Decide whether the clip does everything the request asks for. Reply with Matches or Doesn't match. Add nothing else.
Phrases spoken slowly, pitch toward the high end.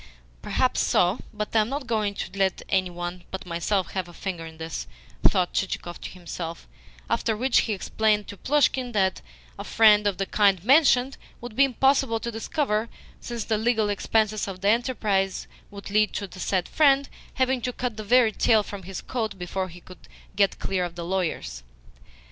Doesn't match